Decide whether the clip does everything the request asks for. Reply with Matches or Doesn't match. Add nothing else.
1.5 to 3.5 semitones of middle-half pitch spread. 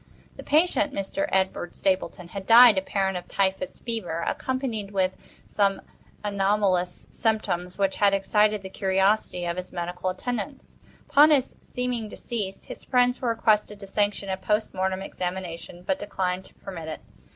Matches